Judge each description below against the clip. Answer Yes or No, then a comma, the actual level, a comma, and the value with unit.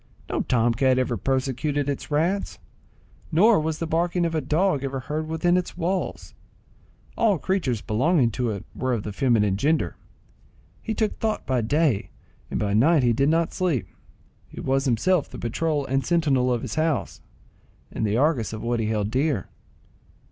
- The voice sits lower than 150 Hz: Yes, medium, 140 Hz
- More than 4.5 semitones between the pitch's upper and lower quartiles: Yes, wide, 5.6 semitones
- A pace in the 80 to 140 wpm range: No, average, 175 wpm